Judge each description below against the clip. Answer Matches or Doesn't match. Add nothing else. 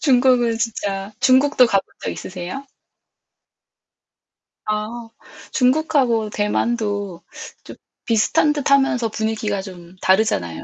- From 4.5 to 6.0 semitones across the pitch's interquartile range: Doesn't match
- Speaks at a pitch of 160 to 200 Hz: Doesn't match